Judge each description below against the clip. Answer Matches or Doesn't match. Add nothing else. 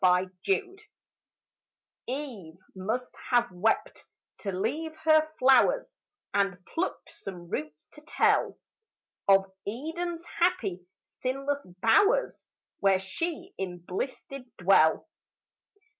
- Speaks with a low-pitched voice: Doesn't match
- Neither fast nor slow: Doesn't match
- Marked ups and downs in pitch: Matches